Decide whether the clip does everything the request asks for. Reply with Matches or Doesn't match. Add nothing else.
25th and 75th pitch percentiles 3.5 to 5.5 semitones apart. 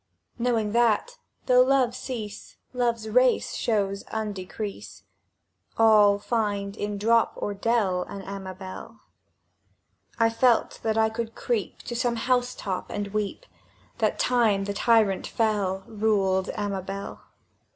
Doesn't match